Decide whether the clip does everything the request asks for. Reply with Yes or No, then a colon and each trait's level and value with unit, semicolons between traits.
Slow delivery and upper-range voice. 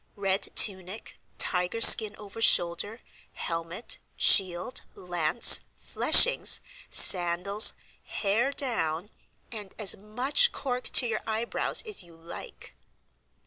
Yes: slow, 100 wpm; high, 200 Hz